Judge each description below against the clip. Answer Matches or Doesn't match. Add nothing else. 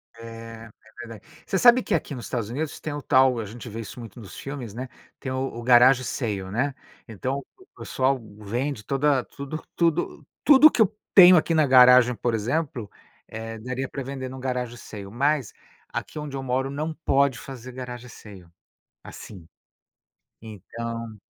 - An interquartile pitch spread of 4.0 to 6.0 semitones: Doesn't match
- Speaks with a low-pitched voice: Matches